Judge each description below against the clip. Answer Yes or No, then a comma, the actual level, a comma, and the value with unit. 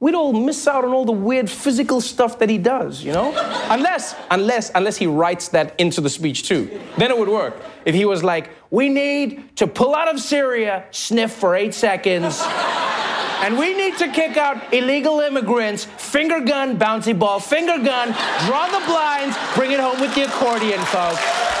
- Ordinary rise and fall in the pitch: No, wide, 5.7 semitones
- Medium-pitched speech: No, very high, 250 Hz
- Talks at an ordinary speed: Yes, average, 190 wpm